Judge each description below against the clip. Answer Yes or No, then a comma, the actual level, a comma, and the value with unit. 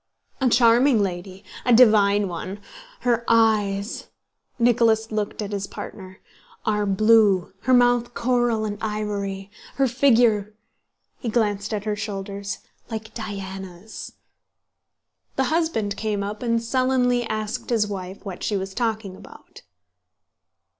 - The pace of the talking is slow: Yes, slow, 125 wpm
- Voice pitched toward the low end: No, high, 215 Hz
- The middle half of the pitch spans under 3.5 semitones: Yes, average, 2.8 semitones